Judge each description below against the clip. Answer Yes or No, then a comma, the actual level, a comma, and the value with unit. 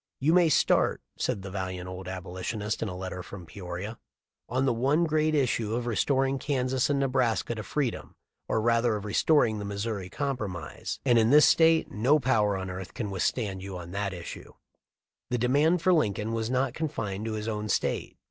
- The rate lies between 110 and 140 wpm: No, average, 185 wpm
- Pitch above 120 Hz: No, low, 110 Hz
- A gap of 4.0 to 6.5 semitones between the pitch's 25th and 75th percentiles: Yes, average, 5.2 semitones